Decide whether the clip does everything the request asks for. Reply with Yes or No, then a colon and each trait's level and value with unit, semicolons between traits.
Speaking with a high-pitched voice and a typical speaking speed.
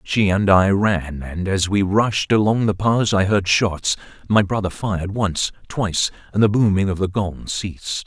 No: low, 100 Hz; average, 170 wpm